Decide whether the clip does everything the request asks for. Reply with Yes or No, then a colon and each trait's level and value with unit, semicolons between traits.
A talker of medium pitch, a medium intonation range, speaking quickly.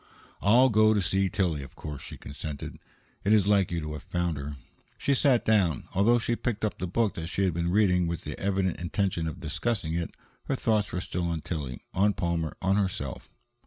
No: very low, 90 Hz; average, 4.0 semitones; fast, 210 wpm